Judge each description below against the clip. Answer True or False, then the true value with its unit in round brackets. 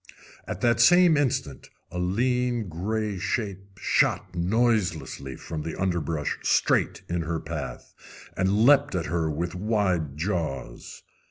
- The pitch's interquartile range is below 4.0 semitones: False (5.3 semitones)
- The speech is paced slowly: True (125 wpm)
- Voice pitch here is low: True (90 Hz)